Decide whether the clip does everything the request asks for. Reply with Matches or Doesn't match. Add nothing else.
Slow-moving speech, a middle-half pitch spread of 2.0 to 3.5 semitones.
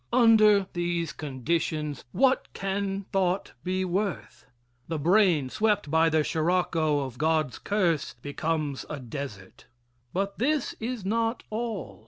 Doesn't match